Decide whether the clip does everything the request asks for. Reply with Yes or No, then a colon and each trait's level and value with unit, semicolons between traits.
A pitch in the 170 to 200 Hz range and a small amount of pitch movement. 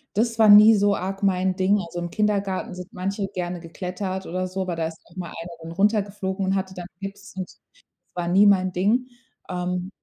Yes: high, 190 Hz; narrow, 1.9 semitones